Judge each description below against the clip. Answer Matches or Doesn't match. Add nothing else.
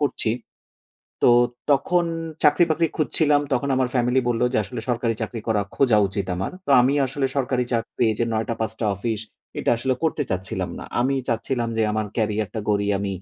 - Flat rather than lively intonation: Doesn't match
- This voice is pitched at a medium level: Doesn't match